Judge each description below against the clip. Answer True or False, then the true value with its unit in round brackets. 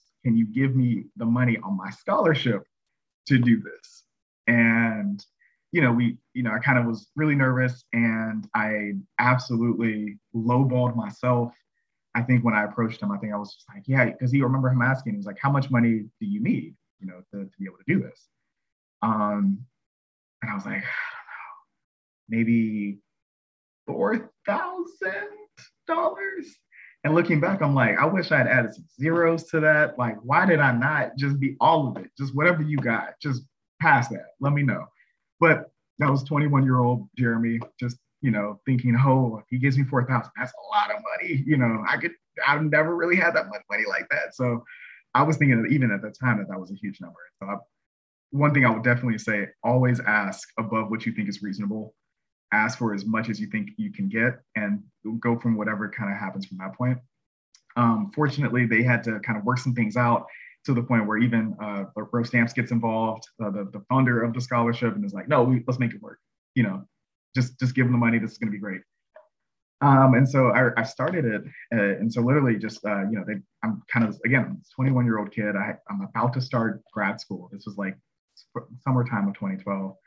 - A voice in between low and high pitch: False (120 Hz)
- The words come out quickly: True (215 wpm)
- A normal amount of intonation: True (3.9 semitones)